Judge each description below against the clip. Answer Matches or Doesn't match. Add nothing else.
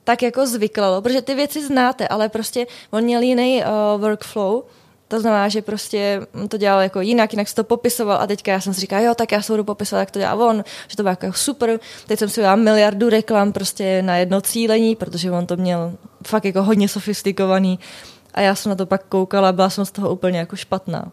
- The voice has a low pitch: Doesn't match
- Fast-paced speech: Matches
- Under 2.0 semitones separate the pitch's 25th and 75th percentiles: Doesn't match